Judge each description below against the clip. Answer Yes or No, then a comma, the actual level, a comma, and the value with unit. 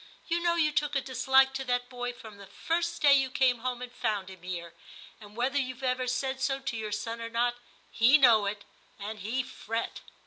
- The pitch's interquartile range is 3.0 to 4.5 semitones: Yes, average, 3.4 semitones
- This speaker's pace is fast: Yes, fast, 215 wpm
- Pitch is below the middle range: No, high, 245 Hz